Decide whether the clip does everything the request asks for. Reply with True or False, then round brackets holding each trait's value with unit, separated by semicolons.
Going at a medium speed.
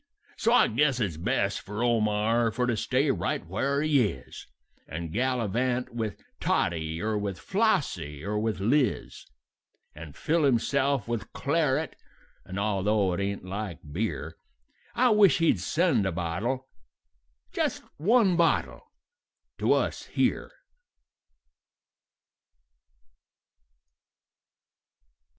False (110 wpm)